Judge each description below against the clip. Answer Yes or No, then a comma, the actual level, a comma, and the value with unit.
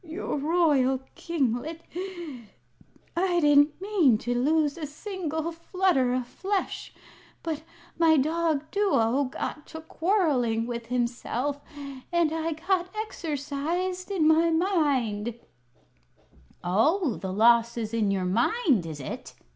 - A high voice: Yes, very high, 300 Hz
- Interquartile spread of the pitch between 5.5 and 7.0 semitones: Yes, wide, 5.8 semitones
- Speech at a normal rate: No, slow, 120 wpm